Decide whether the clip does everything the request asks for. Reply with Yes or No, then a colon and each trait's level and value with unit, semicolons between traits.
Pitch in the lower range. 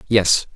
Yes: very low, 95 Hz